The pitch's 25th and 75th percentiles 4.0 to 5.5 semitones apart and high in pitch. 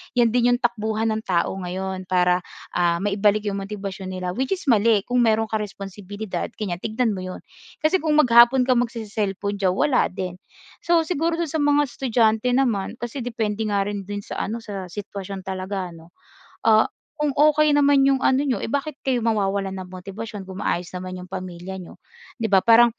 Yes: average, 4.4 semitones; high, 215 Hz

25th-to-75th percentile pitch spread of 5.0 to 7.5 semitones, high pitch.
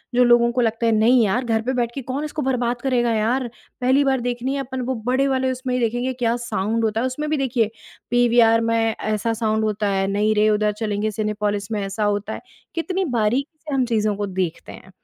No: average, 3.1 semitones; high, 235 Hz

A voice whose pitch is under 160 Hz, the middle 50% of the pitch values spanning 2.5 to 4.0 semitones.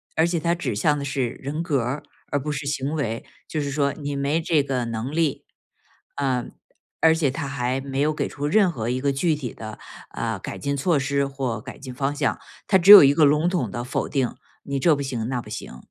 Yes: medium, 140 Hz; average, 2.9 semitones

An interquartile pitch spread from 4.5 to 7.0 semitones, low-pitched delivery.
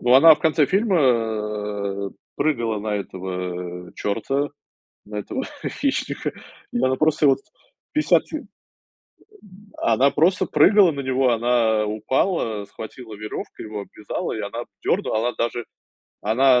Yes: average, 4.8 semitones; low, 115 Hz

